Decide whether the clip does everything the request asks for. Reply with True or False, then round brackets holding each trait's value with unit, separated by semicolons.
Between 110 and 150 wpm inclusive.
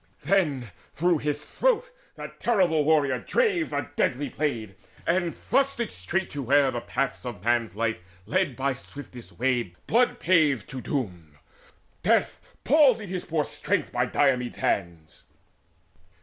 True (140 wpm)